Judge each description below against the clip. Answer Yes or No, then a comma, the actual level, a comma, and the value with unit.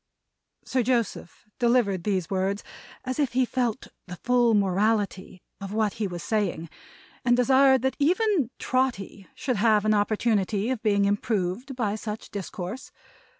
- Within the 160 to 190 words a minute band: No, average, 145 wpm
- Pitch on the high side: Yes, high, 220 Hz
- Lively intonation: No, average, 4.0 semitones